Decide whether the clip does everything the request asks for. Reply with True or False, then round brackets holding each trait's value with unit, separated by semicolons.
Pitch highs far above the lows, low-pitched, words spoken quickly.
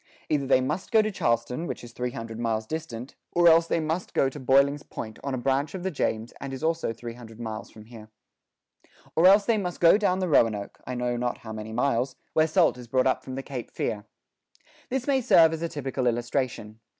True (5.7 semitones; 130 Hz; 225 wpm)